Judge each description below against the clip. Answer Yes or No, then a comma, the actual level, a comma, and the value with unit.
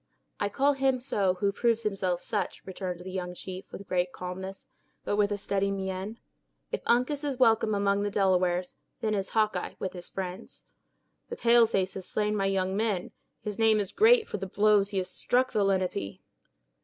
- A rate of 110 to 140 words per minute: No, average, 190 wpm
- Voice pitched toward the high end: Yes, high, 200 Hz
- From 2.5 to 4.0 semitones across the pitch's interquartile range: Yes, average, 2.8 semitones